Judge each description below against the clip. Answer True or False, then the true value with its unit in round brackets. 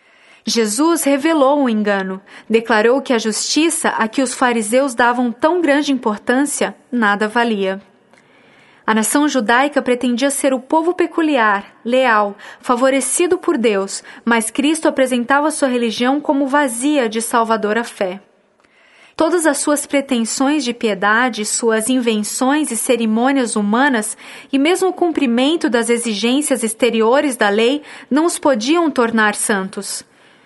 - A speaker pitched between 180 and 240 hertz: False (250 Hz)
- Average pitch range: True (4.1 semitones)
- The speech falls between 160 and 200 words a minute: False (130 wpm)